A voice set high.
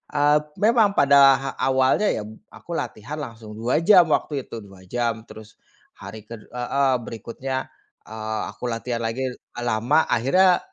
No: low, 120 Hz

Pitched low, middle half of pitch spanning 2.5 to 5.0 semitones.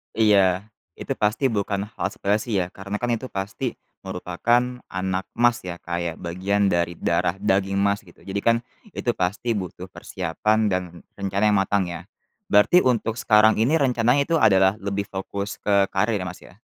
Yes: low, 100 Hz; average, 3.0 semitones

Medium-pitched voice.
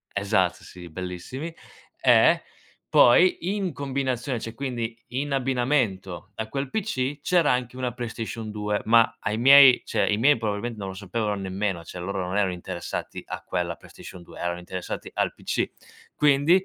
No: low, 115 Hz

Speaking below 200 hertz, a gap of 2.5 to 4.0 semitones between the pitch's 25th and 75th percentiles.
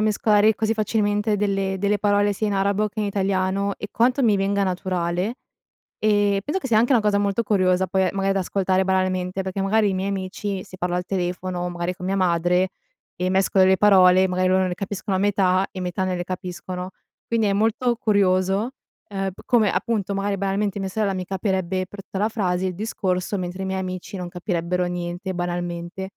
No: high, 190 Hz; narrow, 1.9 semitones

